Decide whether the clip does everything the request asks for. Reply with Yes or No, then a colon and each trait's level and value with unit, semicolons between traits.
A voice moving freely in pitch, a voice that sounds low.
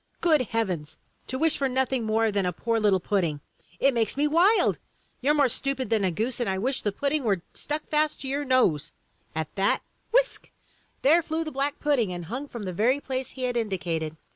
No: wide, 6.3 semitones; very high, 250 Hz